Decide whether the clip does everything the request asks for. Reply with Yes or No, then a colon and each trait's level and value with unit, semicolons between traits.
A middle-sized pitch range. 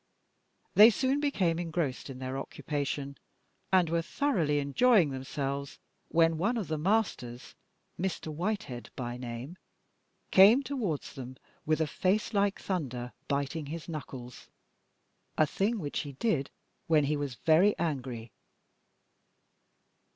No: wide, 5.8 semitones